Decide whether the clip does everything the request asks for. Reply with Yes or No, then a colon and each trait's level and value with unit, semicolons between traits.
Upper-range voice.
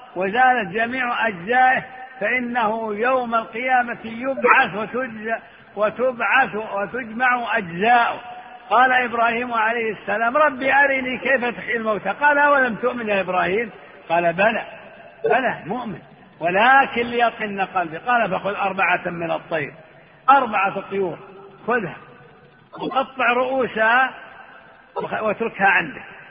Yes: high, 230 Hz